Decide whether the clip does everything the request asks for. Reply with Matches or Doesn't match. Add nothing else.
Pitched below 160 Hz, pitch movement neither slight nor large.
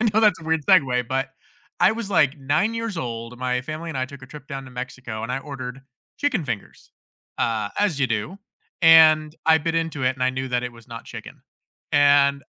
Matches